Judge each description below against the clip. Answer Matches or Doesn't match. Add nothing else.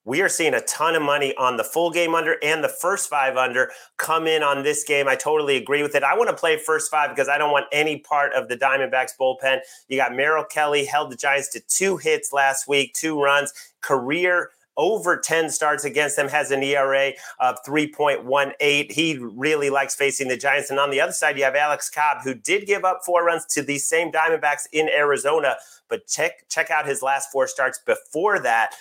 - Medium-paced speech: Doesn't match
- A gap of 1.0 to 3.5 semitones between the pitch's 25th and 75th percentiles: Matches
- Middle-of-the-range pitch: Matches